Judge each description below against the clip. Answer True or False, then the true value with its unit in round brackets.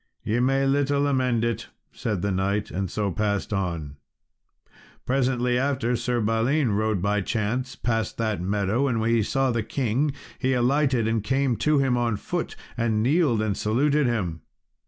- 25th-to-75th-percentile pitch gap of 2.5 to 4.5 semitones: True (4.0 semitones)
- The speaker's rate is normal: True (165 wpm)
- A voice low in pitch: True (115 Hz)